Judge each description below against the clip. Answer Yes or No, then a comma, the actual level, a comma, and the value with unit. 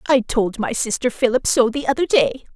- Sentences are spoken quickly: Yes, fast, 210 wpm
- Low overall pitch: No, very high, 250 Hz